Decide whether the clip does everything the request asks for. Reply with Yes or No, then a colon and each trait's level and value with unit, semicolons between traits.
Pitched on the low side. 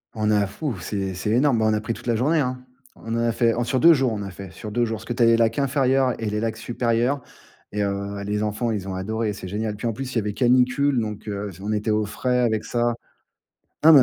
Yes: low, 115 Hz